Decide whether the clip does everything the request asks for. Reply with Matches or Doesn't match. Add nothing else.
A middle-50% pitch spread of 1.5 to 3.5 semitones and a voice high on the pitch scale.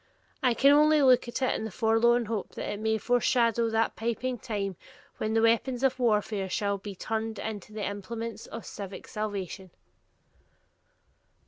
Matches